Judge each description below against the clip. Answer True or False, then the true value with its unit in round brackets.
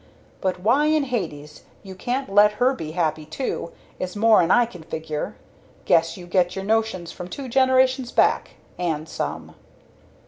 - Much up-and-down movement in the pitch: True (6.7 semitones)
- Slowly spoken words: False (160 wpm)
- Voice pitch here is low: False (195 Hz)